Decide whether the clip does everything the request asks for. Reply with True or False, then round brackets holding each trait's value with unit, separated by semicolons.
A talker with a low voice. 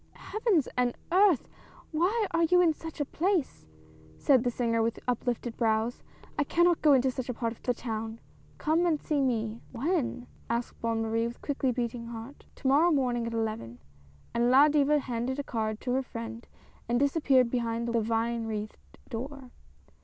False (245 Hz)